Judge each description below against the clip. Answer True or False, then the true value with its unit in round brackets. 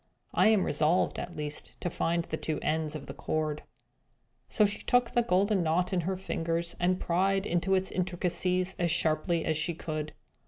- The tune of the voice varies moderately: True (3.0 semitones)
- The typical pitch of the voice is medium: True (175 Hz)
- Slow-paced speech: False (185 wpm)